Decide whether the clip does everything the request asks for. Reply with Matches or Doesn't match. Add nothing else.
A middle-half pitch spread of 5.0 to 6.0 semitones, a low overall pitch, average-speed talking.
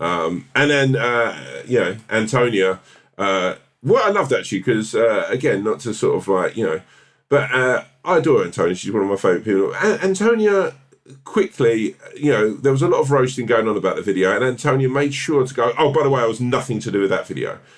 Doesn't match